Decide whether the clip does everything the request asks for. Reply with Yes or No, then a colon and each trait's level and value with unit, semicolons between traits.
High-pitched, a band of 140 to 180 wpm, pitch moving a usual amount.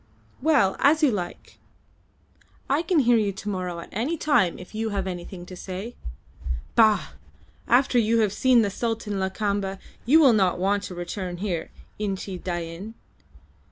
Yes: high, 205 Hz; average, 160 wpm; average, 4.1 semitones